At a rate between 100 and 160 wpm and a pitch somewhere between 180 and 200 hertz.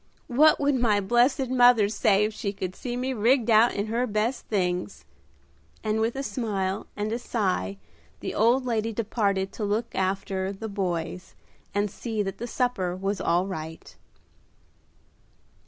No: average, 155 wpm; high, 215 Hz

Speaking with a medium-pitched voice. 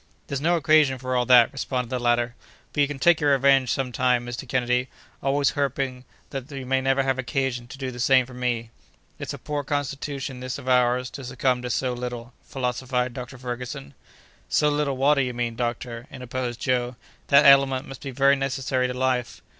No: low, 130 Hz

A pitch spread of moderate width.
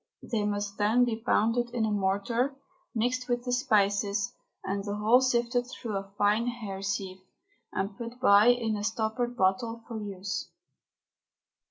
Yes: average, 3.2 semitones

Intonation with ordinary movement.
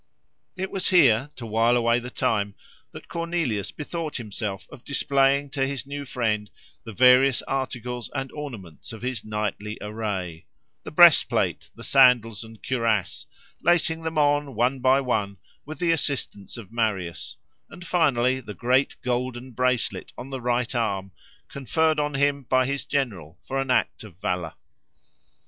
Yes: average, 4.3 semitones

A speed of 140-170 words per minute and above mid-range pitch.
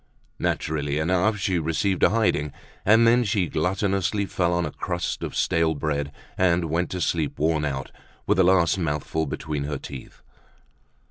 No: average, 160 wpm; very low, 85 Hz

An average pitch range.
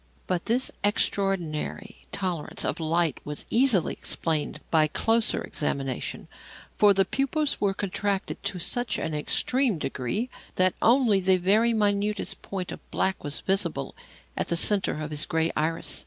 Yes: average, 4.6 semitones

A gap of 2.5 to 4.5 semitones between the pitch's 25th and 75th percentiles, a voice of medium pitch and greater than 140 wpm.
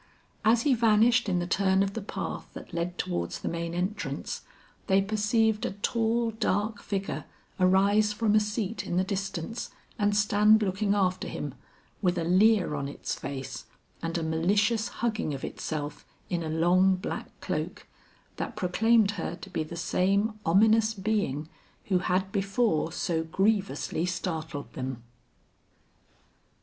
No: average, 4.0 semitones; high, 195 Hz; average, 150 wpm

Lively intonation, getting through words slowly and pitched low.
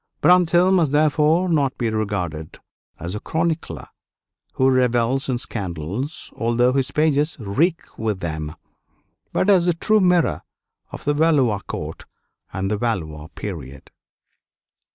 Yes: wide, 8.1 semitones; slow, 130 wpm; low, 130 Hz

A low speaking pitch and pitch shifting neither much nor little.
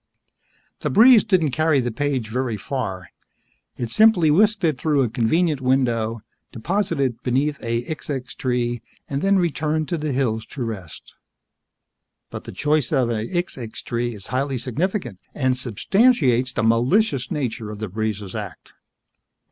Yes: low, 130 Hz; average, 5.0 semitones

